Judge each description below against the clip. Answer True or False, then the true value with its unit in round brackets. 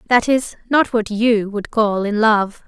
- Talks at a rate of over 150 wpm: True (200 wpm)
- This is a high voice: True (220 Hz)